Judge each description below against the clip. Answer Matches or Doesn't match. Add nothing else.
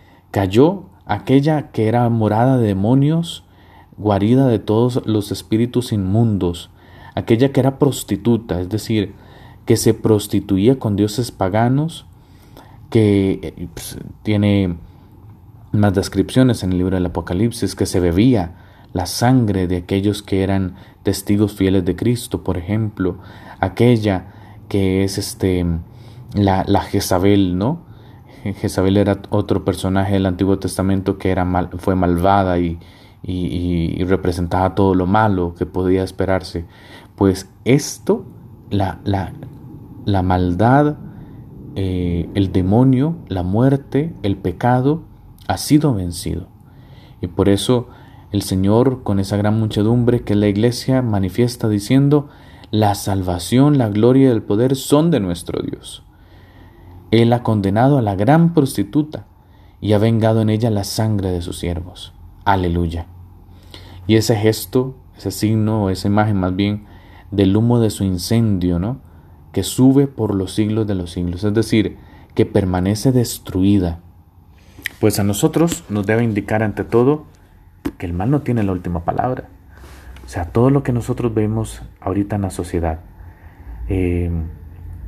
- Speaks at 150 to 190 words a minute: Doesn't match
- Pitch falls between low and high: Doesn't match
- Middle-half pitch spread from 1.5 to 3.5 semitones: Doesn't match